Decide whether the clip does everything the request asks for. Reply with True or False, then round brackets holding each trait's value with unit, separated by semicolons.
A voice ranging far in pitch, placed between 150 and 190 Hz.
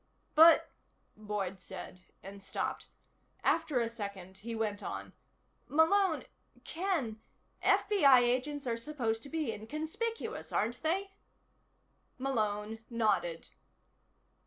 False (6.9 semitones; 235 Hz)